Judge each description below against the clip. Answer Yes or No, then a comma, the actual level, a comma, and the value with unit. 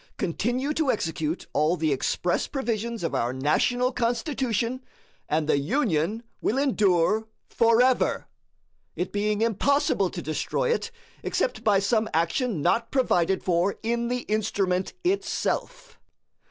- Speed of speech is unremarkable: No, slow, 125 wpm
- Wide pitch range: Yes, wide, 6.2 semitones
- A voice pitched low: No, high, 220 Hz